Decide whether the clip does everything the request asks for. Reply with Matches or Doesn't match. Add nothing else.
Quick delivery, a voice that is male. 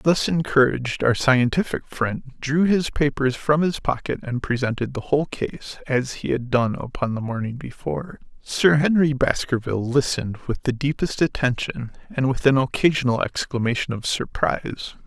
Doesn't match